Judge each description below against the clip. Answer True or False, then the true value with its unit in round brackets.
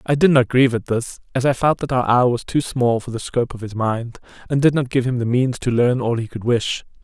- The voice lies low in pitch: True (125 Hz)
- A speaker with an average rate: False (290 wpm)